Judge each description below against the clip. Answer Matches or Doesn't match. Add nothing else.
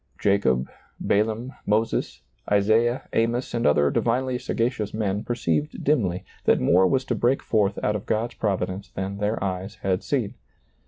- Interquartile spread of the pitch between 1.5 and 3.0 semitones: Doesn't match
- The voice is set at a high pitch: Doesn't match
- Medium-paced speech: Matches